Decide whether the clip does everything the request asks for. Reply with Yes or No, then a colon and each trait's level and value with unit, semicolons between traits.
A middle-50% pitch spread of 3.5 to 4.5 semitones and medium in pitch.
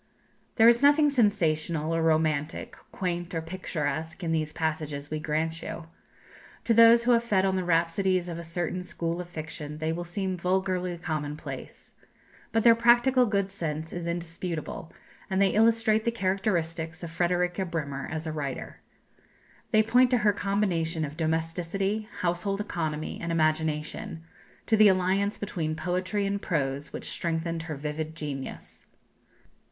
Yes: average, 3.9 semitones; medium, 170 Hz